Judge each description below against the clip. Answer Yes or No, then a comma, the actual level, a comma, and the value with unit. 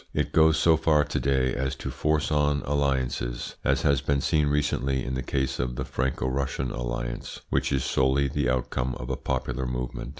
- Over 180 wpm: Yes, average, 195 wpm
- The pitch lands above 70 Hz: No, very low, 65 Hz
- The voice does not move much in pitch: Yes, narrow, 2.3 semitones